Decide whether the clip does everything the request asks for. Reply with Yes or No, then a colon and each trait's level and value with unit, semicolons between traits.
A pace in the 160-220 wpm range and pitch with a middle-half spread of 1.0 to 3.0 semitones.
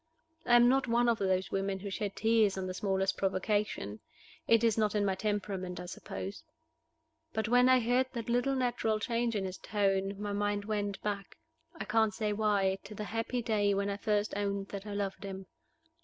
Yes: average, 200 wpm; narrow, 2.4 semitones